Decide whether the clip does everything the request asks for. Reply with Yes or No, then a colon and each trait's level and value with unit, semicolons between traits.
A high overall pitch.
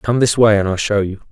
No: low, 105 Hz